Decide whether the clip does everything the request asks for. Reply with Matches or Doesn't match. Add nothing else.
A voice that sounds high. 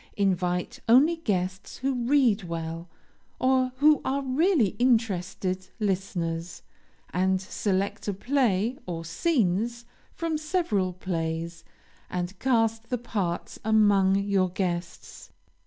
Matches